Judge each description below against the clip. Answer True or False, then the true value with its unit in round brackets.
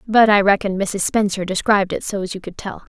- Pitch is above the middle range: True (200 Hz)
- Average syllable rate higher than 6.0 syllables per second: False (5.5 syllables/s)